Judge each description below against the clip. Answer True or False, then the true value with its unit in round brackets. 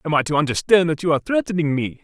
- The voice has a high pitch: False (160 Hz)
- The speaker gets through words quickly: True (265 wpm)